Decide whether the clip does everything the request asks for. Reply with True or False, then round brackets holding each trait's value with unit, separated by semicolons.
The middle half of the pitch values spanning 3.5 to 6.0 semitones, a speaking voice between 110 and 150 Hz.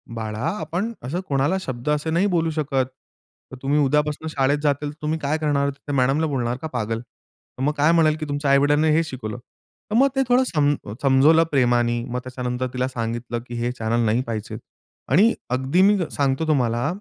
True (3.8 semitones; 140 Hz)